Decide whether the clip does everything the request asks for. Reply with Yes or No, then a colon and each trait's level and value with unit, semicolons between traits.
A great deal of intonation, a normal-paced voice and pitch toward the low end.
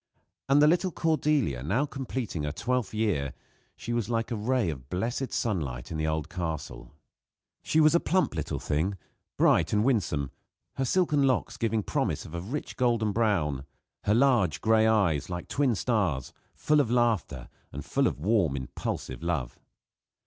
Yes: wide, 8.1 semitones; average, 165 wpm; low, 110 Hz